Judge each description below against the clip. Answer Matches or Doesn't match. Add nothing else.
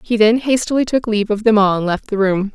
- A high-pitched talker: Matches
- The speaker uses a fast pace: Matches